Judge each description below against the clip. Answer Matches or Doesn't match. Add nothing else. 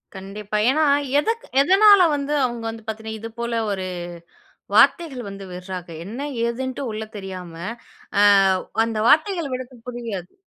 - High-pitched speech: Matches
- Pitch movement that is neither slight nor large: Doesn't match